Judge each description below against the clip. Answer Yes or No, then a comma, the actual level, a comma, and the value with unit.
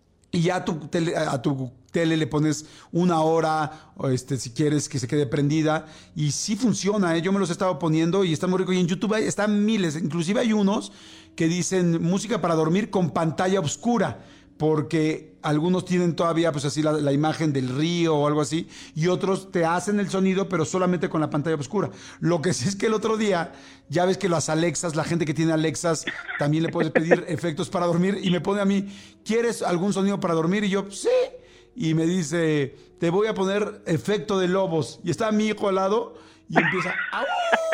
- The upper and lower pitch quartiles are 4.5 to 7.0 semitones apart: No, average, 3.7 semitones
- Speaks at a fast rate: Yes, fast, 210 wpm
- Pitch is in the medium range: Yes, medium, 170 Hz